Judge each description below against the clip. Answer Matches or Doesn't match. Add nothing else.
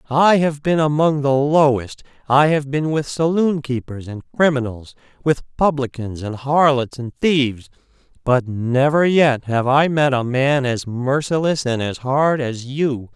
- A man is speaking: Matches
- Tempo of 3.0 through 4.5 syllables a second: Matches